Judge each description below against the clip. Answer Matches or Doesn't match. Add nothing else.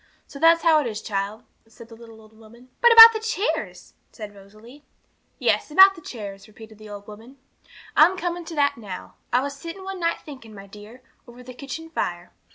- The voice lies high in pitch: Matches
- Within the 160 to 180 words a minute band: Doesn't match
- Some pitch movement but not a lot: Doesn't match